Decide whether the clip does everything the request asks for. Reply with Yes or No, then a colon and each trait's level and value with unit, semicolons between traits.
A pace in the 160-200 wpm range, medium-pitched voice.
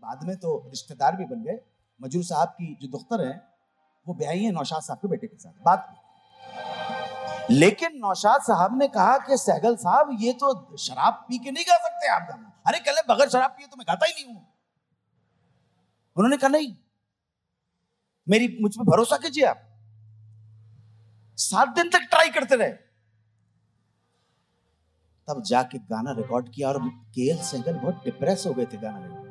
Yes: average, 170 wpm; medium, 180 Hz